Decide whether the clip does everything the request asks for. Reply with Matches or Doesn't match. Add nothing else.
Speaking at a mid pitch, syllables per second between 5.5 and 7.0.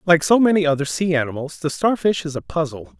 Matches